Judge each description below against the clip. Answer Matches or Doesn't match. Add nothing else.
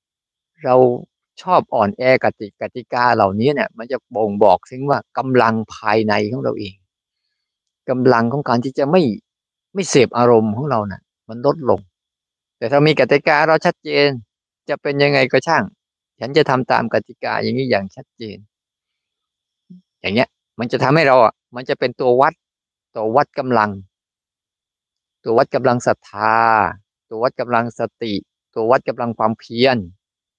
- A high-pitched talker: Doesn't match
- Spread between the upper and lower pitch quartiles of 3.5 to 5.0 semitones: Matches